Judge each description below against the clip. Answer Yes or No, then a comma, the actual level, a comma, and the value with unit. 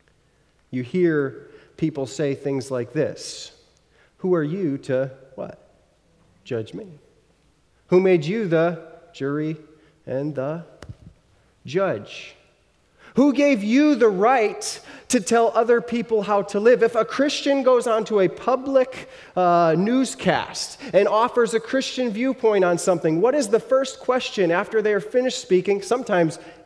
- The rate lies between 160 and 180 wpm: No, slow, 135 wpm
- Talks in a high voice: Yes, high, 205 Hz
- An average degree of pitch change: No, wide, 6.9 semitones